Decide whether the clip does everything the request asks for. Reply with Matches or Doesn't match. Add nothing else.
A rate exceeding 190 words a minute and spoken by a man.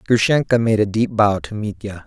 Matches